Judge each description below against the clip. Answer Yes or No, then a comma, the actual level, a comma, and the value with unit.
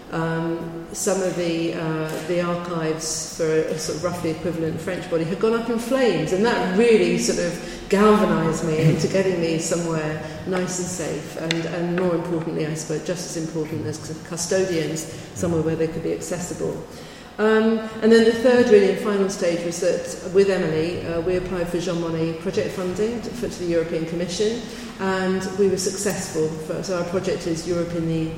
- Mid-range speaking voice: Yes, medium, 175 Hz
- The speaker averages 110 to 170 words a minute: No, average, 190 wpm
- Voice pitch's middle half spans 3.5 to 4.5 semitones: No, average, 2.9 semitones